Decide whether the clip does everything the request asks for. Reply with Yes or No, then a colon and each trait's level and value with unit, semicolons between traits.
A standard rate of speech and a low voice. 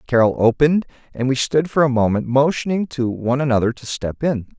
Yes: average, 195 wpm; low, 130 Hz